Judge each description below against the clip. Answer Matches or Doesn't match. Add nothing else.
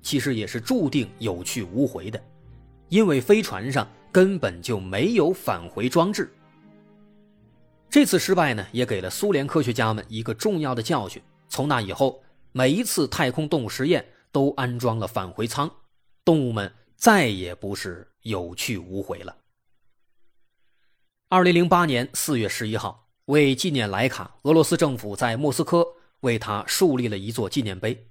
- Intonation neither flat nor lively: Doesn't match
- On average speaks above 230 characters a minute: Matches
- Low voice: Matches